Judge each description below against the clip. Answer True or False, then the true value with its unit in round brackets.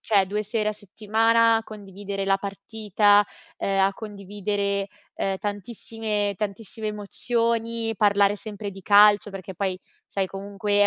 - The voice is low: False (205 Hz)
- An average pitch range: False (1.6 semitones)